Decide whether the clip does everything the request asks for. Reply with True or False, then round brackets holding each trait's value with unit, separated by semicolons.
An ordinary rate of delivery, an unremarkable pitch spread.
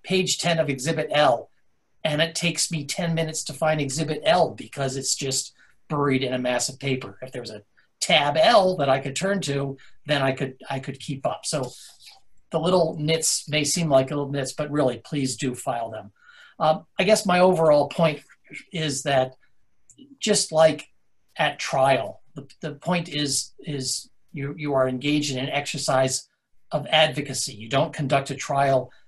True (180 wpm; 3.2 semitones)